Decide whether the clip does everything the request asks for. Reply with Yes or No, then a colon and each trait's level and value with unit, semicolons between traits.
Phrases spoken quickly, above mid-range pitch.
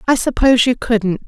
No: average, 190 wpm; high, 230 Hz